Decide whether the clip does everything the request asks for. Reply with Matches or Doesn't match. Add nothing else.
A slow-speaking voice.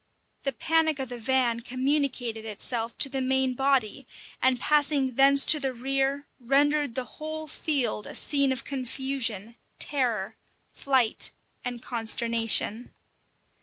Matches